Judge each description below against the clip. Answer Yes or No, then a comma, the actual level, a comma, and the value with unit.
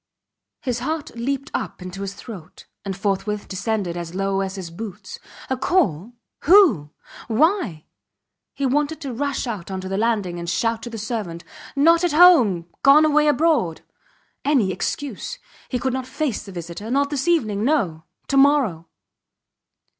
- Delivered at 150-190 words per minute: Yes, average, 155 wpm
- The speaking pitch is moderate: No, high, 230 Hz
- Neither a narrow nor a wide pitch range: No, wide, 7.0 semitones